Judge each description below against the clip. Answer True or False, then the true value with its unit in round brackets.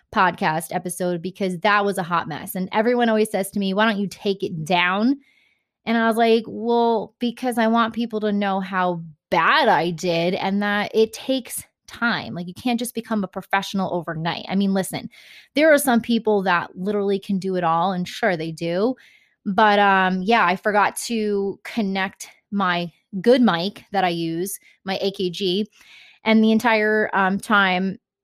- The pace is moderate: True (180 wpm)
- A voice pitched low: False (200 Hz)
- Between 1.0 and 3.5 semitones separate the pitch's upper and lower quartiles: True (3.2 semitones)